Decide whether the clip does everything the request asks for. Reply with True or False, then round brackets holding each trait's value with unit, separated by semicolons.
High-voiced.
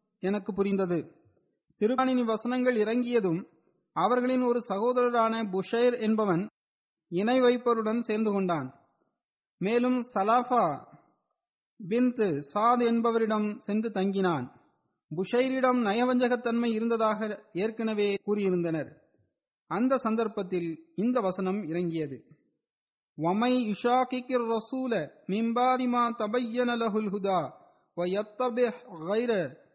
True (220 Hz)